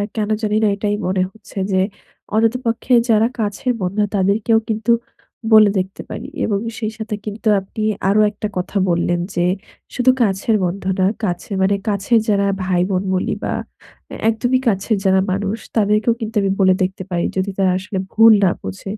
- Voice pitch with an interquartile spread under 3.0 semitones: Yes, narrow, 2.6 semitones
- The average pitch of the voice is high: Yes, high, 205 Hz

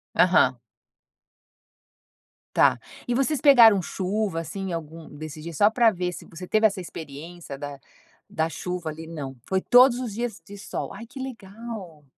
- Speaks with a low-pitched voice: No, medium, 185 Hz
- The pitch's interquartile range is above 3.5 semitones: Yes, wide, 5.6 semitones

